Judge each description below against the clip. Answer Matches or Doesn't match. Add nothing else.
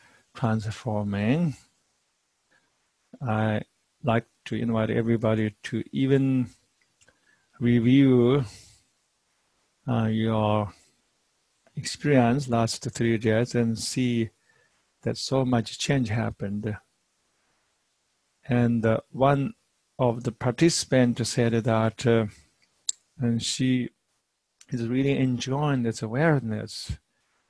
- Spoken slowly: Matches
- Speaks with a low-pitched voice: Matches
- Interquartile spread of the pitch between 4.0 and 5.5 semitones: Doesn't match